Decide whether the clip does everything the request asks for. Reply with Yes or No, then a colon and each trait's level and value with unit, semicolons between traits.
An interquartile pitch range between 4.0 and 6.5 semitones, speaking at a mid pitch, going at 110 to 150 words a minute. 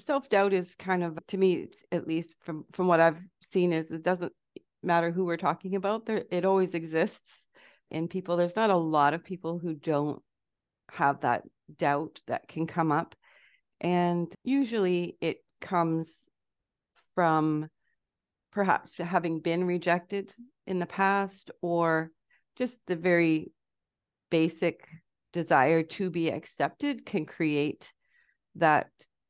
No: average, 2.7 semitones; medium, 175 Hz; slow, 135 wpm